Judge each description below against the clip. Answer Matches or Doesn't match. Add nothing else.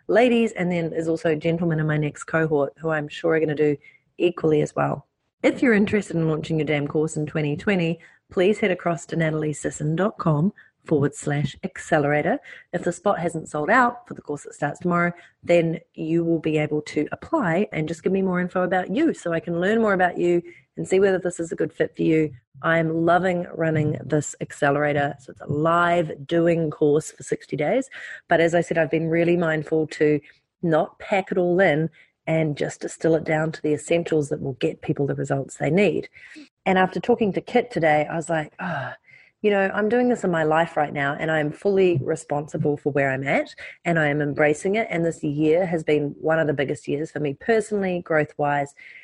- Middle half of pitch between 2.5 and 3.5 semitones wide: Matches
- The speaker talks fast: Matches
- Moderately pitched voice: Matches